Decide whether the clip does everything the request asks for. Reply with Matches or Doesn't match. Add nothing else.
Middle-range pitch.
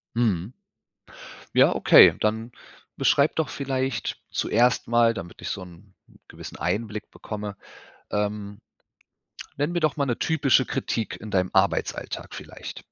Doesn't match